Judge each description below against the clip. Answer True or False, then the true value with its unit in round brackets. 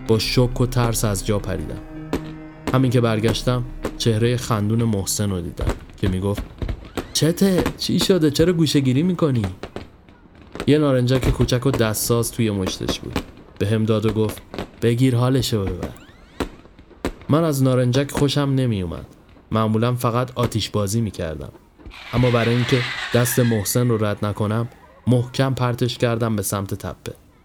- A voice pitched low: True (115 Hz)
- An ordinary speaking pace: True (145 wpm)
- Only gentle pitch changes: False (3.9 semitones)